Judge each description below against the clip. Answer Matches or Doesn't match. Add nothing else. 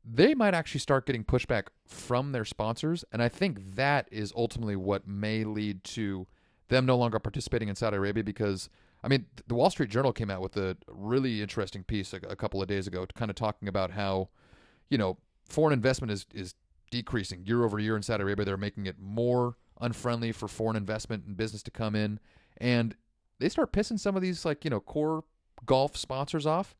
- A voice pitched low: Matches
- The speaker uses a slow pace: Doesn't match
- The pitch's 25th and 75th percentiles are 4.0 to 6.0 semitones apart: Matches